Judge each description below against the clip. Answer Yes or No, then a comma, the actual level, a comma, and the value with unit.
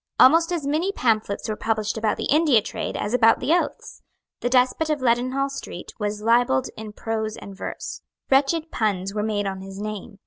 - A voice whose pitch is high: Yes, high, 225 Hz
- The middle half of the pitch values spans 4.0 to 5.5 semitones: Yes, average, 4.7 semitones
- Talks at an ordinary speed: Yes, average, 185 wpm